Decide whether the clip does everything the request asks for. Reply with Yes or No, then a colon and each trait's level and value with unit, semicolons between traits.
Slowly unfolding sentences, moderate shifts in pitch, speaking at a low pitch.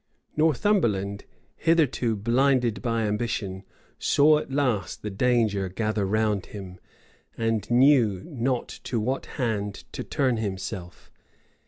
Yes: slow, 115 wpm; average, 4.2 semitones; low, 115 Hz